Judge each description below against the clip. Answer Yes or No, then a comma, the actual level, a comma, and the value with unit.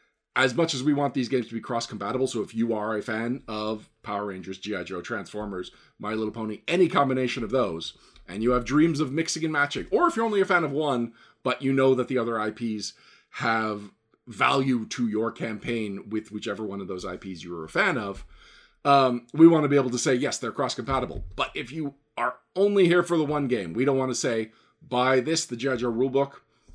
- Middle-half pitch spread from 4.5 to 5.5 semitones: Yes, average, 4.8 semitones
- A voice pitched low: Yes, low, 125 Hz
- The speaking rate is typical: No, fast, 225 wpm